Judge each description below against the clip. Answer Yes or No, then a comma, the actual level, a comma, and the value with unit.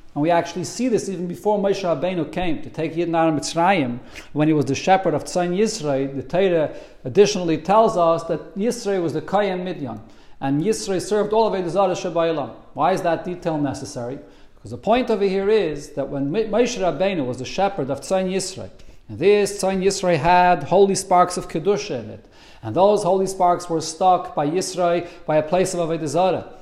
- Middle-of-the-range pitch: Yes, medium, 175 Hz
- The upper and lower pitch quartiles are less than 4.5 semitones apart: Yes, average, 3.9 semitones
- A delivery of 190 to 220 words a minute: Yes, average, 195 wpm